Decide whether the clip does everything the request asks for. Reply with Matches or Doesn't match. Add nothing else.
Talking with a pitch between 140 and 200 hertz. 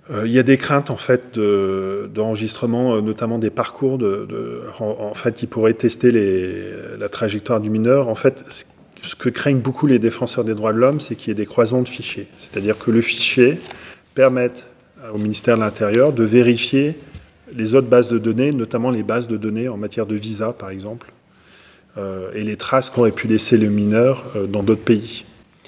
Doesn't match